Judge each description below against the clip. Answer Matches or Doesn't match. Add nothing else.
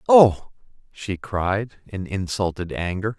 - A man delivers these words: Matches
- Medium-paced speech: Doesn't match